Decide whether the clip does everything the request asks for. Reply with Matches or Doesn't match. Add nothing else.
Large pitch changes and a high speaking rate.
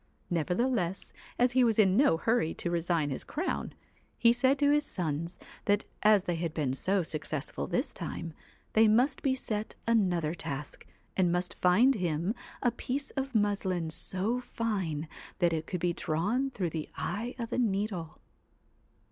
Doesn't match